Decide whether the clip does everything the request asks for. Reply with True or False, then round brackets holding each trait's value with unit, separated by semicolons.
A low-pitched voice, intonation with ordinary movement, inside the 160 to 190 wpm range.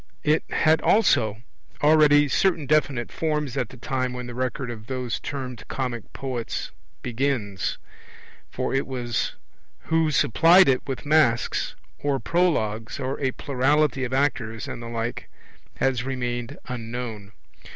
False (130 Hz; 3.4 semitones; 135 wpm)